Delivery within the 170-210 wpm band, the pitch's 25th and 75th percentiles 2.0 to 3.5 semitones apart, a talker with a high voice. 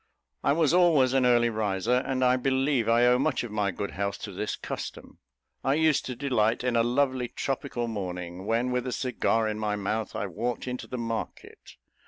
No: average, 195 wpm; average, 3.2 semitones; low, 120 Hz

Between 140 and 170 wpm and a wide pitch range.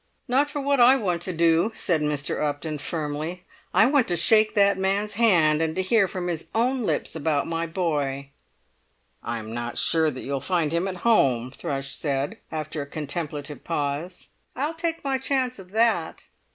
No: average, 180 wpm; wide, 6.5 semitones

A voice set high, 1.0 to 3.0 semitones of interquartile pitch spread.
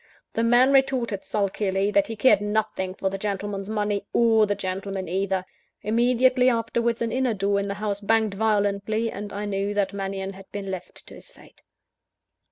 Yes: high, 205 Hz; narrow, 2.4 semitones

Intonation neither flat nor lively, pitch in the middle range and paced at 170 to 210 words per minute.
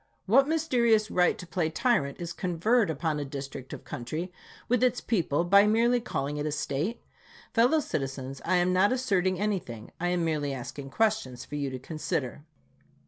No: wide, 7.5 semitones; medium, 175 Hz; average, 175 wpm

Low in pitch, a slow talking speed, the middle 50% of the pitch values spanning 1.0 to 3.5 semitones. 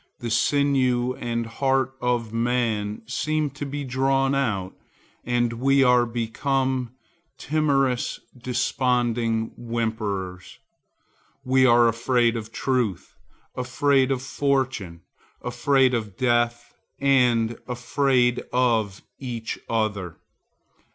Yes: low, 120 Hz; slow, 95 wpm; narrow, 2.5 semitones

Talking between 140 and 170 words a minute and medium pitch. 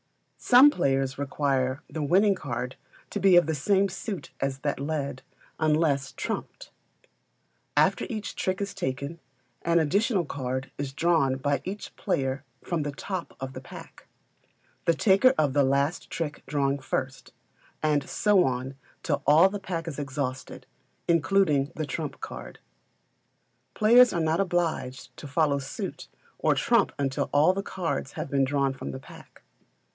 Yes: average, 150 wpm; medium, 145 Hz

